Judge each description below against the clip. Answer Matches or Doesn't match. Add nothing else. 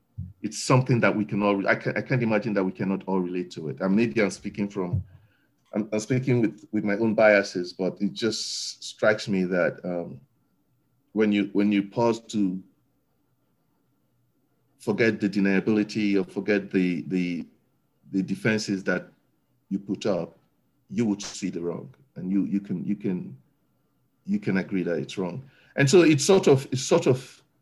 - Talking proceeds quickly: Doesn't match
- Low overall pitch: Matches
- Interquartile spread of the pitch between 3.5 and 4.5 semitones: Doesn't match